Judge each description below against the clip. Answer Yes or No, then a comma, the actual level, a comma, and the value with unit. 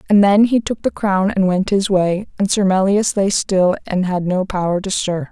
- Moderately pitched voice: No, high, 195 Hz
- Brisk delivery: Yes, fast, 235 wpm